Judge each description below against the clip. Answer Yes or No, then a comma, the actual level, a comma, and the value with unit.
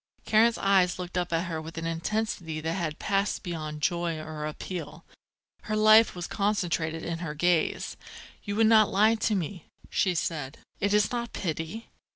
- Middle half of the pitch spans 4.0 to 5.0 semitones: Yes, average, 4.4 semitones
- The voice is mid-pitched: Yes, medium, 175 Hz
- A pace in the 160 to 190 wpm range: Yes, average, 175 wpm